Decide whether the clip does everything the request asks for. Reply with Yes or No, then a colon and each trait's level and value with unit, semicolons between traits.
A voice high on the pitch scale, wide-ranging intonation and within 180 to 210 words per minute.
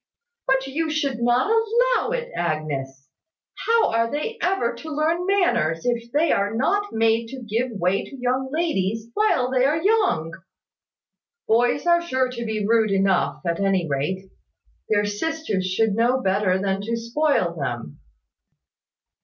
No: high, 235 Hz; wide, 7.8 semitones; average, 150 wpm